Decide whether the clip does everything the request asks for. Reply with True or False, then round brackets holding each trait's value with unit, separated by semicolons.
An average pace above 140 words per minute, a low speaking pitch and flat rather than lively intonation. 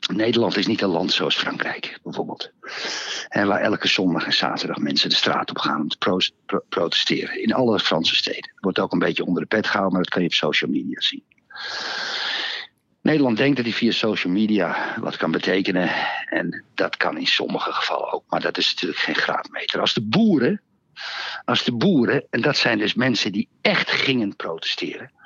True (195 wpm; 110 Hz; 2.3 semitones)